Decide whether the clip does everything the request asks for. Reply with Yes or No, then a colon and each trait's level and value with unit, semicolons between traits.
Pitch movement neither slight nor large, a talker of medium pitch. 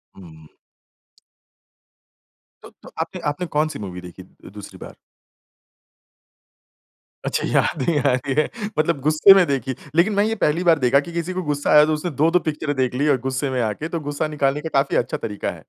Yes: average, 3.8 semitones; medium, 145 Hz